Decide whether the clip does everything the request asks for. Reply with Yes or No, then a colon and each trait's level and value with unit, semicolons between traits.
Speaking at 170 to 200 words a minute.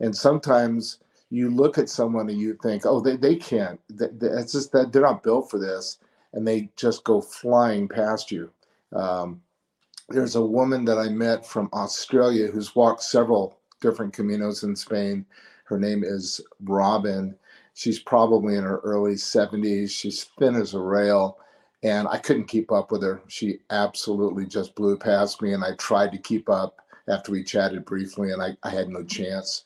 Yes: average, 180 wpm